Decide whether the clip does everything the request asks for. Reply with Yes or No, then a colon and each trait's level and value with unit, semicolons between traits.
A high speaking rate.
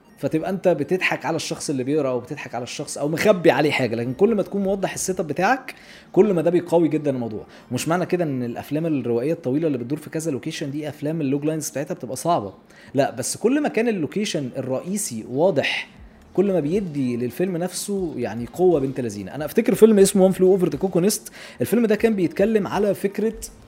Yes: fast, 200 wpm